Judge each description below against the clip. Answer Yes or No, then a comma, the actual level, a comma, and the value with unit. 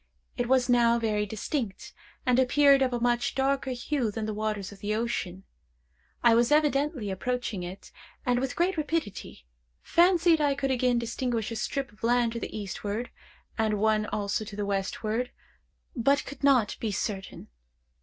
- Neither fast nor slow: Yes, average, 165 wpm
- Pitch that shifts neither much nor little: Yes, average, 4.0 semitones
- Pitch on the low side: No, high, 235 Hz